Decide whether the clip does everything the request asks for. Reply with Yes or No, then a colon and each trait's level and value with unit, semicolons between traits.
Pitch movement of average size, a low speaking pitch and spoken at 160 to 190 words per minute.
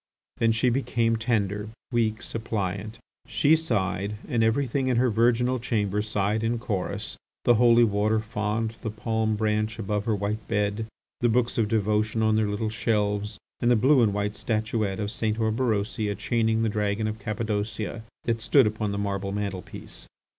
No: narrow, 1.8 semitones; low, 110 Hz; average, 165 wpm